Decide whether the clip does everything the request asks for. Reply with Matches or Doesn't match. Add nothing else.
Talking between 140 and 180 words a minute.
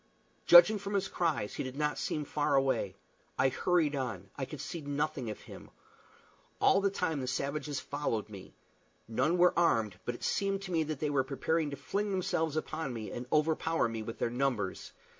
Doesn't match